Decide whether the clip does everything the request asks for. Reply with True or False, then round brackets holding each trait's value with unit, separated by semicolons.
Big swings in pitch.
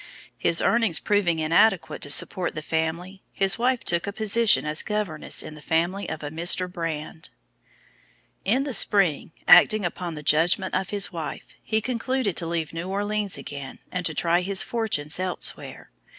False (4.3 semitones)